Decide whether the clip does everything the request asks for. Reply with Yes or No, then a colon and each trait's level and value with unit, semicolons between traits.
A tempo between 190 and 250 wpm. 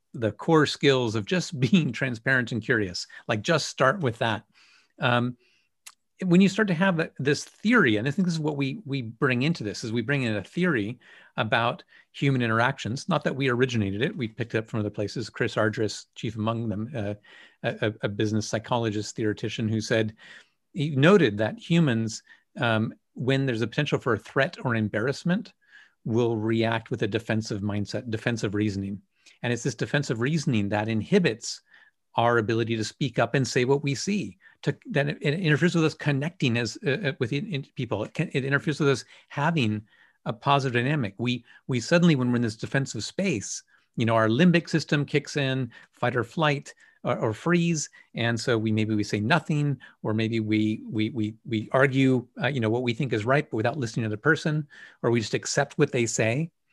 Yes: average, 195 wpm